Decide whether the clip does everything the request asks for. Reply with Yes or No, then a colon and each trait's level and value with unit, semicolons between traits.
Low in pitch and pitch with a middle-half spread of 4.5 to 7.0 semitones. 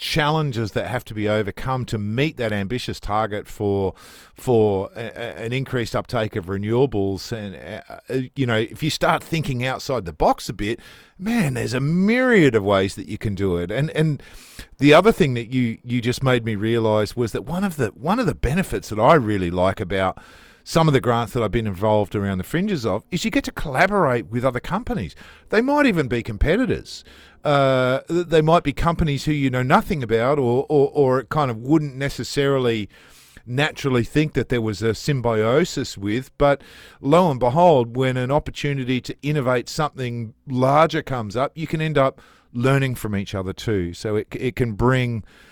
Yes: low, 125 Hz; average, 5.1 semitones